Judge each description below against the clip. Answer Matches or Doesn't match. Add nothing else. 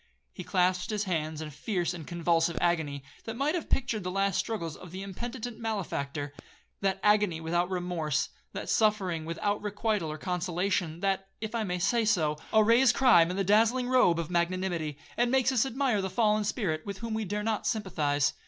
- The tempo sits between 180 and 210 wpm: Matches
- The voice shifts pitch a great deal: Doesn't match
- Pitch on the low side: Doesn't match